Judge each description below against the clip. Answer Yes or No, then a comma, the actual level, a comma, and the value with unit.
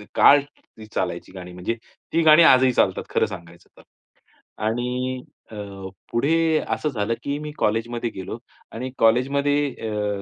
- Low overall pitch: Yes, low, 120 Hz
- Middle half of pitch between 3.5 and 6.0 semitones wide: Yes, average, 5.2 semitones